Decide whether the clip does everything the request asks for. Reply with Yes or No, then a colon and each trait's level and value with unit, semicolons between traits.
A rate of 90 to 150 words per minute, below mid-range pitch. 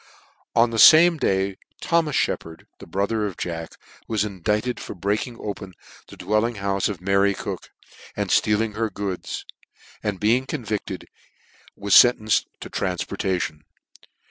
Yes: average, 140 wpm; low, 105 Hz